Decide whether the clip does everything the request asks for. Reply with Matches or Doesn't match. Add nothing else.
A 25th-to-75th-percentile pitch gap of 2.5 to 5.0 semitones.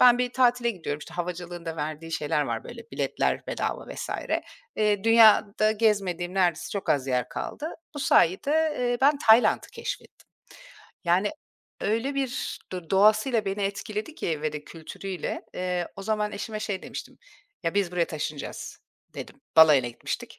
Doesn't match